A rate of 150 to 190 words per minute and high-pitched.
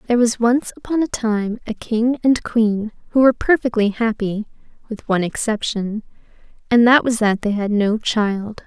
Yes: average, 175 wpm; high, 225 Hz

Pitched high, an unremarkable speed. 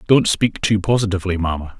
No: low, 100 Hz; average, 165 wpm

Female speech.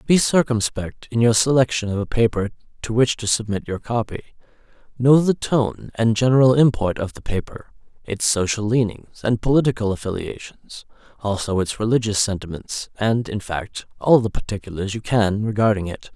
No: male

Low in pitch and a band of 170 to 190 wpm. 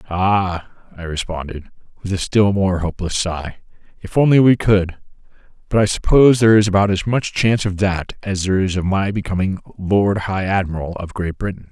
Yes: very low, 95 Hz; average, 185 wpm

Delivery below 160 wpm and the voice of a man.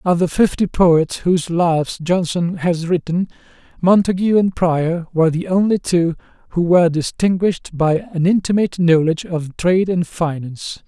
Yes: average, 150 wpm; male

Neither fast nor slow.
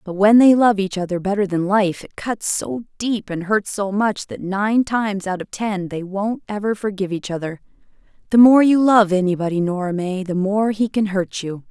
No: fast, 215 wpm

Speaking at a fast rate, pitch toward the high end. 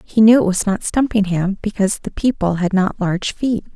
Yes: fast, 210 wpm; high, 200 Hz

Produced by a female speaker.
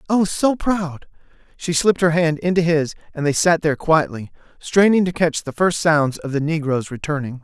No: male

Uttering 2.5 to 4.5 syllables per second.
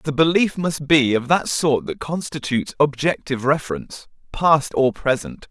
No: 4.8 syllables/s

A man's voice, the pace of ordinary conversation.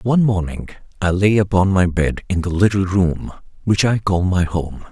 Yes: male; average, 195 wpm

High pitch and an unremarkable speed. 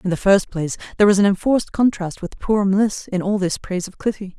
No: high, 195 Hz; fast, 245 wpm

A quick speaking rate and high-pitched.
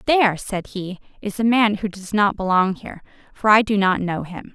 Yes: fast, 225 wpm; high, 200 Hz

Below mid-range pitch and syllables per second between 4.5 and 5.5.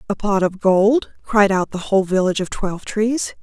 No: high, 200 Hz; 5.1 syllables/s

